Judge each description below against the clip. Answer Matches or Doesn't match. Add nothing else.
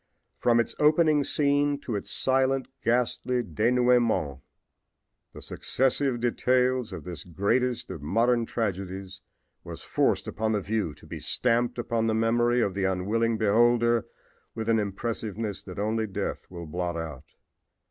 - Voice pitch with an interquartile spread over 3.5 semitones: Matches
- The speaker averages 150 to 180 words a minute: Doesn't match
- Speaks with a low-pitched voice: Matches